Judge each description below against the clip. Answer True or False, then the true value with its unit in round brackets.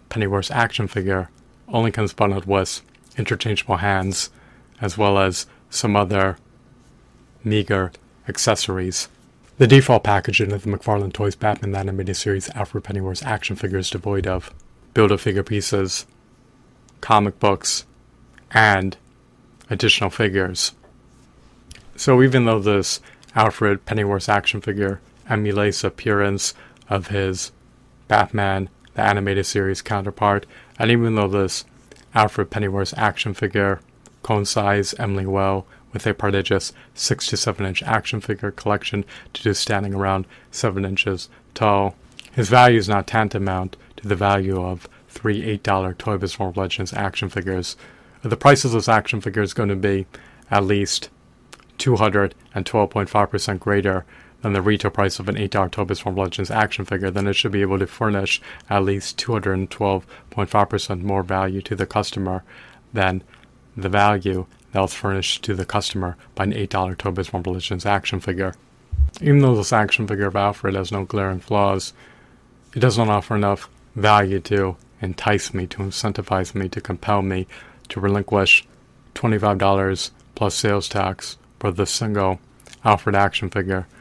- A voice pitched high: False (100 Hz)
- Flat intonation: True (1.9 semitones)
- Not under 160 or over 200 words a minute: False (150 wpm)